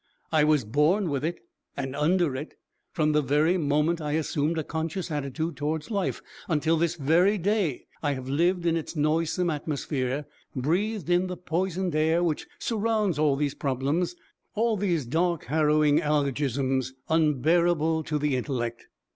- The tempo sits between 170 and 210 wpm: No, average, 155 wpm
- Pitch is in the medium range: Yes, medium, 155 Hz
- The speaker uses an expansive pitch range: No, average, 3.1 semitones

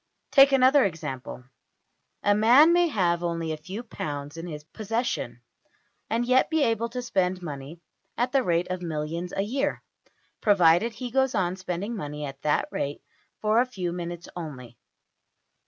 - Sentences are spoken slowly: No, average, 160 wpm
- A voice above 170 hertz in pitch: Yes, medium, 185 Hz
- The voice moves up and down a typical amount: No, wide, 6.5 semitones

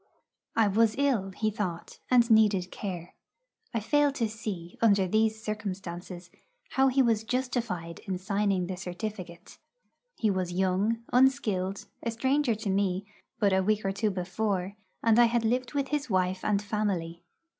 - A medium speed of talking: Yes, average, 155 wpm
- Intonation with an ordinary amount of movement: Yes, average, 3.6 semitones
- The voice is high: Yes, high, 210 Hz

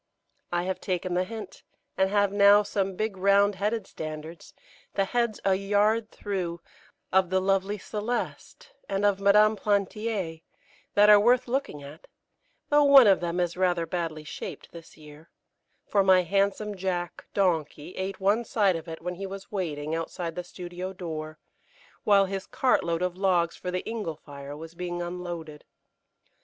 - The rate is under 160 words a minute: No, average, 165 wpm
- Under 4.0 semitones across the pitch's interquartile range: Yes, average, 3.0 semitones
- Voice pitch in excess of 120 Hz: Yes, high, 190 Hz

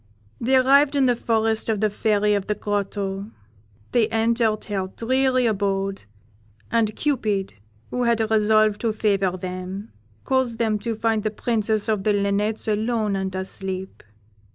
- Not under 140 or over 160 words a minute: Yes, average, 150 wpm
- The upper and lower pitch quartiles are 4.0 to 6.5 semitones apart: No, narrow, 2.4 semitones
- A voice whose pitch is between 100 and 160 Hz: No, high, 215 Hz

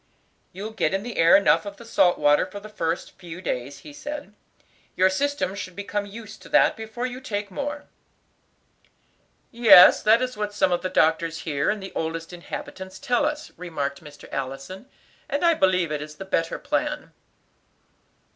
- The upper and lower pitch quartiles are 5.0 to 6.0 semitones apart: Yes, wide, 5.4 semitones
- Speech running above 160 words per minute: Yes, average, 175 wpm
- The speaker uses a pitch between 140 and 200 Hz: Yes, high, 190 Hz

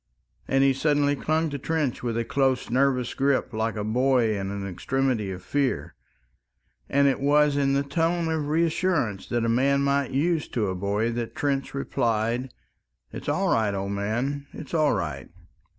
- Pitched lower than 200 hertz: Yes, low, 135 Hz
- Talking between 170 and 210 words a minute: Yes, average, 175 wpm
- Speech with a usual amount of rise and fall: Yes, average, 4.1 semitones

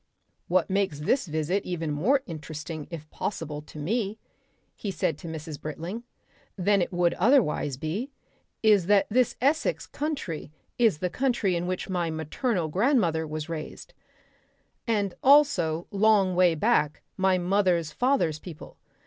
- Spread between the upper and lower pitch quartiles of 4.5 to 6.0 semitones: Yes, average, 5.1 semitones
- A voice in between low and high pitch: Yes, medium, 180 Hz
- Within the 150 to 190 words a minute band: No, average, 140 wpm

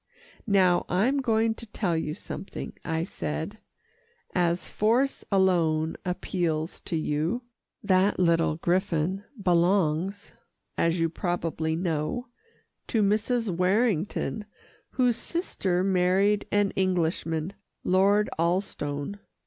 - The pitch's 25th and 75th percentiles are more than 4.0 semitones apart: No, average, 3.7 semitones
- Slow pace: Yes, slow, 100 wpm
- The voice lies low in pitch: No, medium, 185 Hz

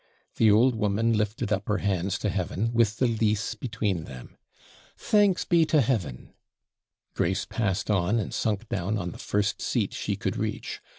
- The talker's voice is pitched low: Yes, low, 105 Hz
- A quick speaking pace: No, average, 170 wpm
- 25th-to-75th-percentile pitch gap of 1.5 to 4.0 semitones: Yes, average, 2.9 semitones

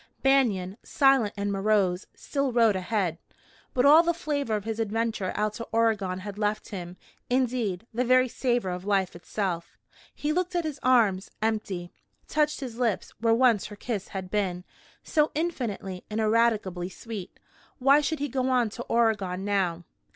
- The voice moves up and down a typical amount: Yes, average, 4.8 semitones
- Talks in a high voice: Yes, high, 220 Hz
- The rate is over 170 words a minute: No, average, 165 wpm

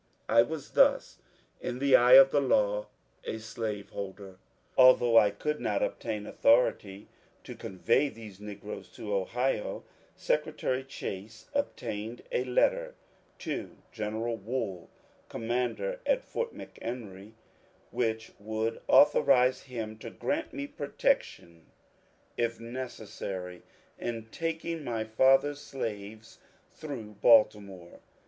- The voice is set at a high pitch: No, low, 115 Hz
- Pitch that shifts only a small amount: No, average, 4.1 semitones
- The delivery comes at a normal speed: No, slow, 110 wpm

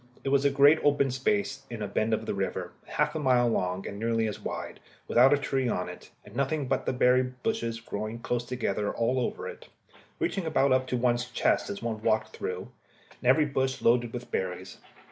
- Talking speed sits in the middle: No, fast, 220 wpm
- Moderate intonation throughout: Yes, average, 3.4 semitones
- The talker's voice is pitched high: No, low, 125 Hz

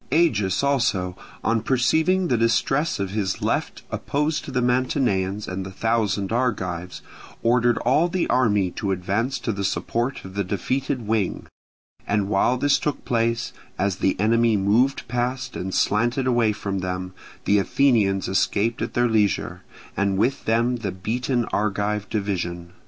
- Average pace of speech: Yes, average, 150 wpm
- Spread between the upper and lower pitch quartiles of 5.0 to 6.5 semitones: No, average, 4.3 semitones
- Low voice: Yes, low, 110 Hz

